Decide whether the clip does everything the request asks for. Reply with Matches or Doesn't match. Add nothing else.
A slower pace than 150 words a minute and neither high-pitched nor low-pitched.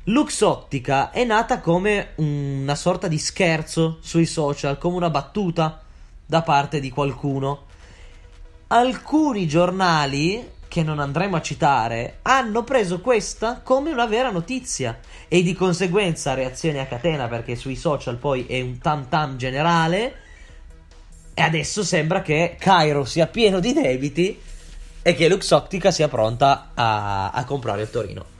Matches